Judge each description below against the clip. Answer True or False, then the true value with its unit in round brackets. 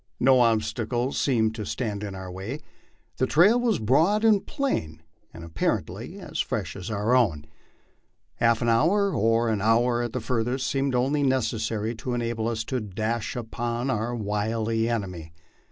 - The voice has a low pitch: True (115 Hz)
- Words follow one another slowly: False (170 wpm)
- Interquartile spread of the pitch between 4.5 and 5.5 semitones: False (3.2 semitones)